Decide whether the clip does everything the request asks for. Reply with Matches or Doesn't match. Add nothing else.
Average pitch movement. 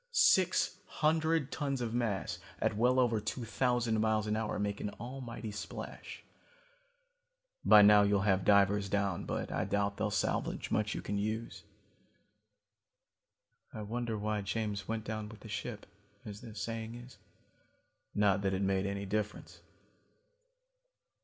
Doesn't match